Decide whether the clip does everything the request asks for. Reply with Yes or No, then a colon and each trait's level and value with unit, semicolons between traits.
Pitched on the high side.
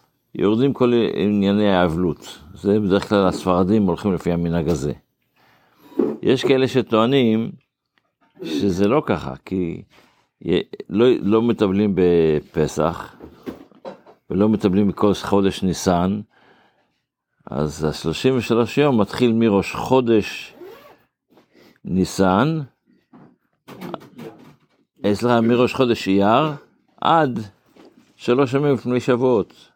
No: low, 105 Hz